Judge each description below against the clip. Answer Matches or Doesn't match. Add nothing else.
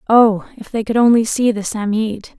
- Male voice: Doesn't match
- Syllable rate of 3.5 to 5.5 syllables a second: Matches